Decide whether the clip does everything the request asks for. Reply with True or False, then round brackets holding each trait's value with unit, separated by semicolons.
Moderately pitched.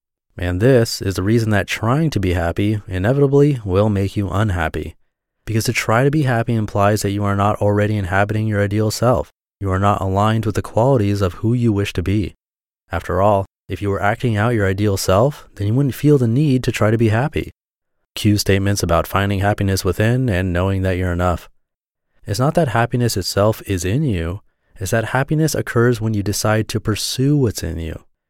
False (105 Hz)